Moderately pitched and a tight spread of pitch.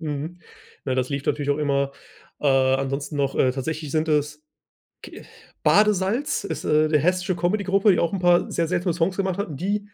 No: medium, 160 Hz; average, 4.6 semitones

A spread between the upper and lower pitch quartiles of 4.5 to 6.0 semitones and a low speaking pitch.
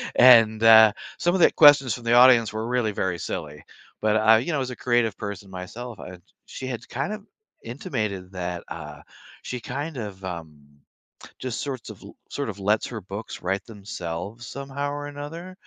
Yes: average, 5.0 semitones; low, 115 Hz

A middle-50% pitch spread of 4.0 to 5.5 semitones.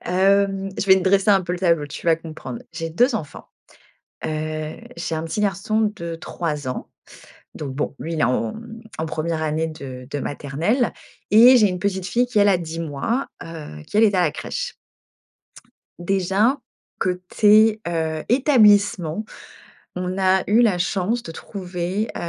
Yes: average, 4.4 semitones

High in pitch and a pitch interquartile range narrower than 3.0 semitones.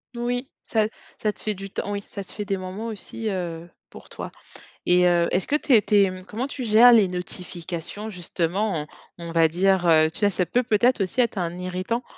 No: high, 195 Hz; average, 3.6 semitones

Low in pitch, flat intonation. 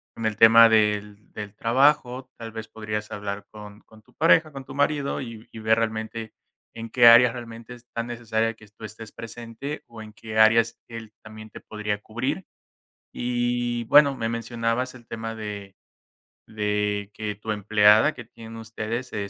Yes: low, 115 Hz; narrow, 1.8 semitones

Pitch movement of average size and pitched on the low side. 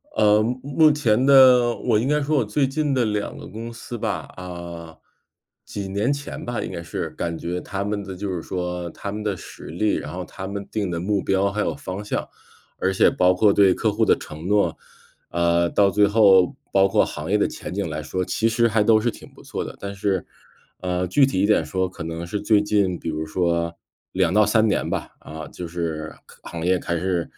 Yes: average, 3.7 semitones; low, 100 Hz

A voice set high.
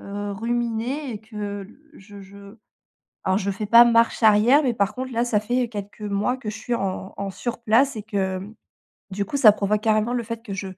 Yes: high, 215 Hz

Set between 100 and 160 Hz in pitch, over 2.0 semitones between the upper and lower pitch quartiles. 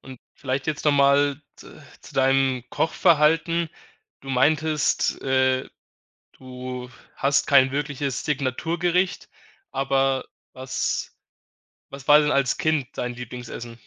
Yes: low, 135 Hz; narrow, 2.4 semitones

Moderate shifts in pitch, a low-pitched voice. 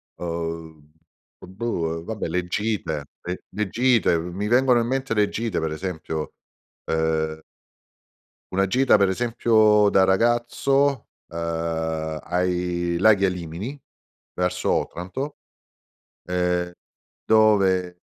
Yes: average, 4.8 semitones; very low, 90 Hz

